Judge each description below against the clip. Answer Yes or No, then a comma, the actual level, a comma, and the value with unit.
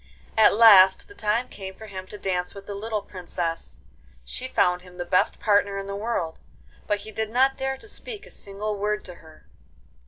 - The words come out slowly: No, fast, 205 wpm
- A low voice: No, high, 200 Hz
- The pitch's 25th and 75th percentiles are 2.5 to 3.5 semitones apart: Yes, average, 2.9 semitones